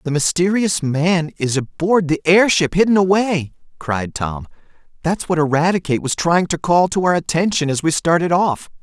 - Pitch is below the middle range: No, medium, 165 Hz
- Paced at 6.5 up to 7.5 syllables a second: No, 4.9 syllables/s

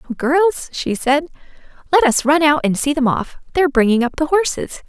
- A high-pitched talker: Yes, very high, 290 Hz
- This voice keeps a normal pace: No, fast, 210 wpm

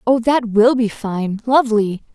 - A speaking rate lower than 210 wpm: Yes, average, 140 wpm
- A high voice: Yes, high, 230 Hz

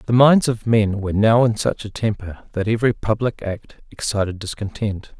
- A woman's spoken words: No, male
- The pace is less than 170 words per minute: No, average, 185 wpm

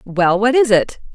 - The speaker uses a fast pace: Yes, fast, 210 wpm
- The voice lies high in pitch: Yes, high, 215 Hz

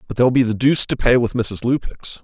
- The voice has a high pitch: No, low, 120 Hz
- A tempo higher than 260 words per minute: Yes, fast, 270 wpm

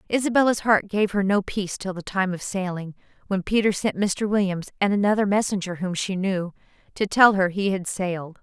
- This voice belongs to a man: No, female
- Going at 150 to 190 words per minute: No, average, 200 wpm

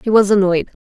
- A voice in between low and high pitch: No, high, 200 Hz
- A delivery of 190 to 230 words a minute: Yes, fast, 220 wpm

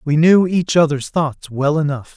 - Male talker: Yes, male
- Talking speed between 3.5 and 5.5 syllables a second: Yes, 4.4 syllables/s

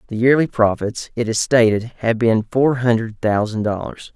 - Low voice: Yes, low, 115 Hz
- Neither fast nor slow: Yes, average, 175 wpm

